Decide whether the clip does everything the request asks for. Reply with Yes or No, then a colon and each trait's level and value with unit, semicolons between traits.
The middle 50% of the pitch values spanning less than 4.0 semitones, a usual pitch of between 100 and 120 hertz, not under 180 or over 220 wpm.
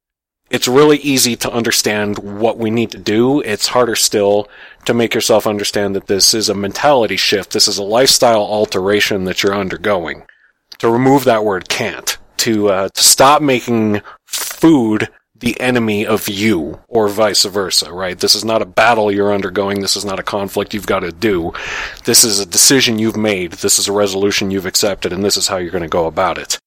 Yes: narrow, 2.5 semitones; low, 105 Hz; average, 200 wpm